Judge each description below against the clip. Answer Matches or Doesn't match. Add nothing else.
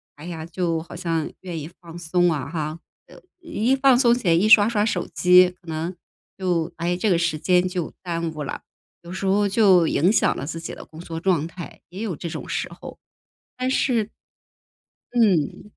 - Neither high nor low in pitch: Matches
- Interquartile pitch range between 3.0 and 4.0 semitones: Matches